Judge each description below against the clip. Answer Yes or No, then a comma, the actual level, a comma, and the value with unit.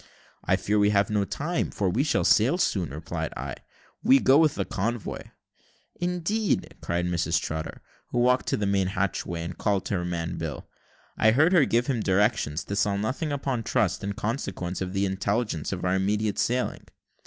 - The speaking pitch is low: Yes, low, 100 Hz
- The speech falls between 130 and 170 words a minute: No, average, 185 wpm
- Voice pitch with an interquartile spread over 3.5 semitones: Yes, wide, 5.4 semitones